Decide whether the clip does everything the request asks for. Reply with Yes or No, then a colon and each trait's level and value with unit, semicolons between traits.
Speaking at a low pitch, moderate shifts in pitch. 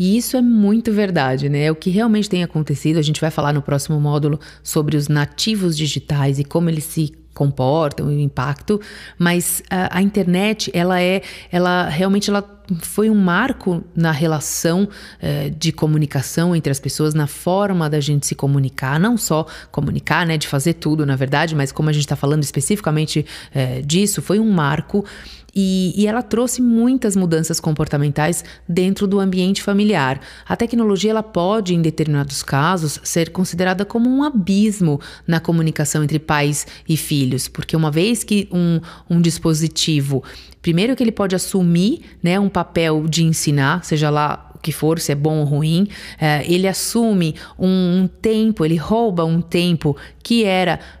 No: medium, 165 Hz; average, 4.4 semitones